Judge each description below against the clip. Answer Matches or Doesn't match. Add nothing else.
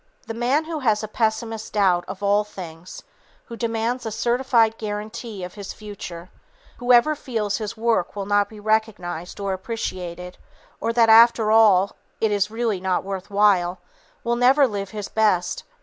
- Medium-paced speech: Matches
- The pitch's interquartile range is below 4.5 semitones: Matches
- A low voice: Doesn't match